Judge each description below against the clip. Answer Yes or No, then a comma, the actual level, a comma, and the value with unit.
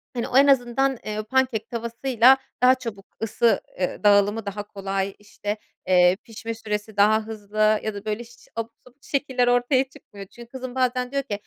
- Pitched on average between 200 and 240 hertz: Yes, high, 225 Hz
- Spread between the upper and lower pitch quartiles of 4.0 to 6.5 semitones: No, average, 3.4 semitones